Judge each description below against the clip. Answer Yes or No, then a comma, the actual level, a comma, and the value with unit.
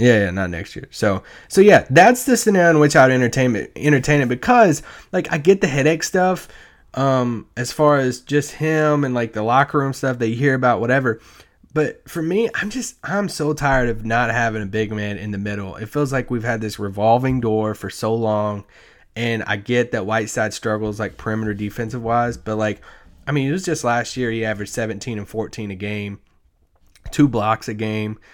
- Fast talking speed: Yes, fast, 210 wpm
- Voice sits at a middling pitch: No, low, 120 Hz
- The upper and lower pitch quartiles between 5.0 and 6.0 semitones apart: Yes, average, 5.3 semitones